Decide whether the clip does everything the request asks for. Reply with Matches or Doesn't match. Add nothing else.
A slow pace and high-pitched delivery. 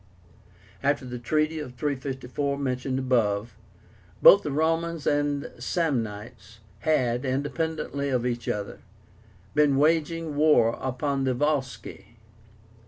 Doesn't match